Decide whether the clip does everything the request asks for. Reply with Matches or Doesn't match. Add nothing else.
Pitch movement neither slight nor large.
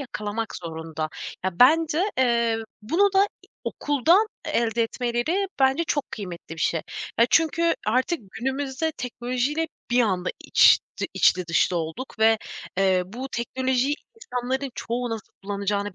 Doesn't match